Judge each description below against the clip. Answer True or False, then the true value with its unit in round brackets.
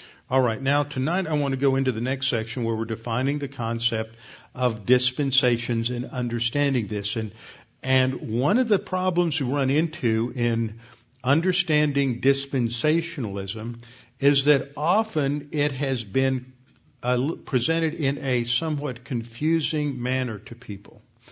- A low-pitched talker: True (130 Hz)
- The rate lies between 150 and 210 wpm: False (140 wpm)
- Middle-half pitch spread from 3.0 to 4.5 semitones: True (3.6 semitones)